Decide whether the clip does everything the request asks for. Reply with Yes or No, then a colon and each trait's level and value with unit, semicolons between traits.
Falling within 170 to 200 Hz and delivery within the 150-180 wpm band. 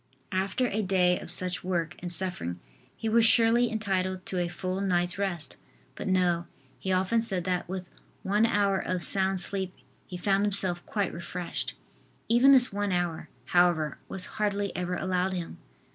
Yes: medium, 185 Hz; average, 165 wpm